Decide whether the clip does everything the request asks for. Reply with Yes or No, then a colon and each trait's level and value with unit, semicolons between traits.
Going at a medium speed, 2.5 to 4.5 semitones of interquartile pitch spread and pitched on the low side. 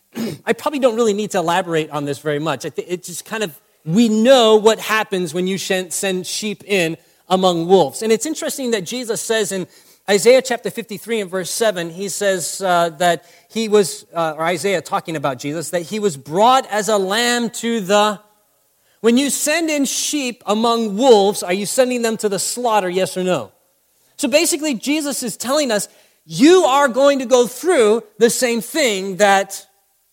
No: average, 185 wpm; average, 4.2 semitones; high, 210 Hz